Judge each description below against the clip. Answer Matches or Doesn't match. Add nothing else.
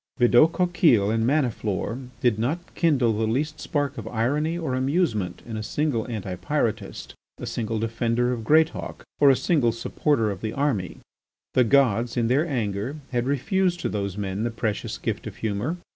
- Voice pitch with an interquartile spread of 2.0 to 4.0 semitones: Doesn't match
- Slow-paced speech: Doesn't match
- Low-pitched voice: Matches